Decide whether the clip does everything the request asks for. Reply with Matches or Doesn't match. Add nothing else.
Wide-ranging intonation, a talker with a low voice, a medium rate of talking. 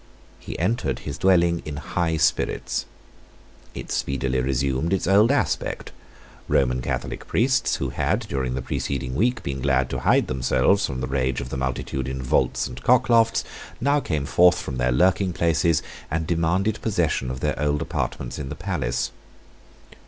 Matches